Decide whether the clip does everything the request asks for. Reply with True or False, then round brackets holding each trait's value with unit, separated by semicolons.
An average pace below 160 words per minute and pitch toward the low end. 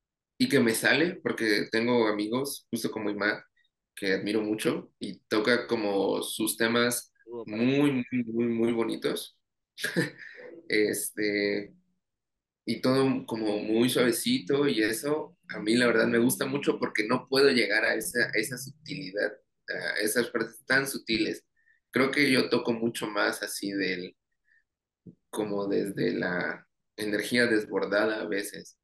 True (140 wpm; 115 Hz)